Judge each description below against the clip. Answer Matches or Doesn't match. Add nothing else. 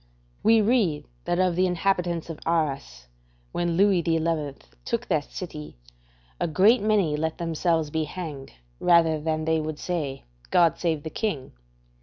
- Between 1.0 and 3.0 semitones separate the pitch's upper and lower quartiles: Matches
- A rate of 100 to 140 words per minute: Doesn't match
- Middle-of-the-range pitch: Matches